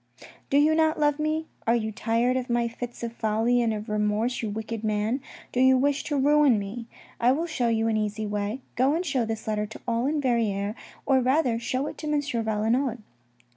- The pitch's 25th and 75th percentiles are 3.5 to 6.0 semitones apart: Yes, average, 3.9 semitones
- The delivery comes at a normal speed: No, fast, 210 wpm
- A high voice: Yes, high, 235 Hz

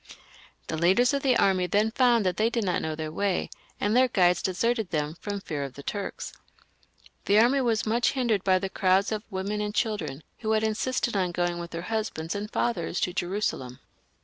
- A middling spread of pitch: Yes, average, 4.0 semitones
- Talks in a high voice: Yes, high, 200 Hz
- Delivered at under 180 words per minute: No, average, 200 wpm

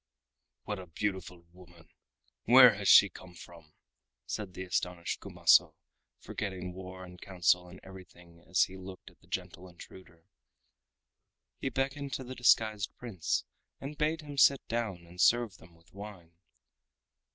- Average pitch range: Yes, average, 4.2 semitones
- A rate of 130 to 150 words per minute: Yes, average, 145 wpm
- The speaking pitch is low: Yes, very low, 95 Hz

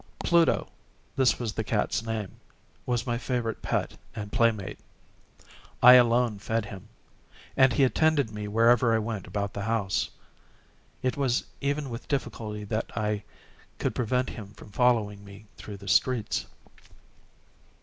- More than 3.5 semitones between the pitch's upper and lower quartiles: No, average, 3.2 semitones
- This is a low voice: Yes, low, 115 Hz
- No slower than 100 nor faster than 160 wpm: Yes, slow, 135 wpm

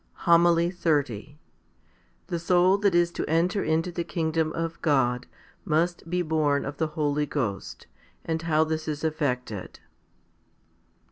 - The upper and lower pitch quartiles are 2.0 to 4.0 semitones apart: Yes, narrow, 2.6 semitones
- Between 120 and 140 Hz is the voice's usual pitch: No, medium, 160 Hz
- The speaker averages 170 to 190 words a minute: No, average, 140 wpm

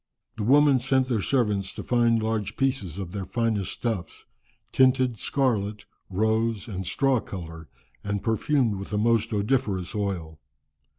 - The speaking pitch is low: Yes, low, 110 Hz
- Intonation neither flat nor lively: Yes, average, 4.1 semitones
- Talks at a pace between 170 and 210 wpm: No, average, 145 wpm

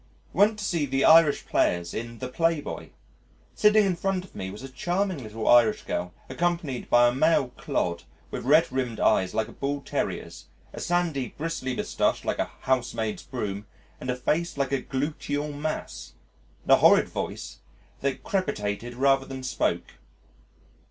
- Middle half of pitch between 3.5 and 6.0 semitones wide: Yes, wide, 5.4 semitones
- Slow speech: No, average, 165 wpm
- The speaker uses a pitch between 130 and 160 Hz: Yes, low, 135 Hz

